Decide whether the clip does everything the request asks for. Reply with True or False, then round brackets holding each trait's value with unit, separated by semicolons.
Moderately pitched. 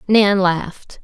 False (195 Hz)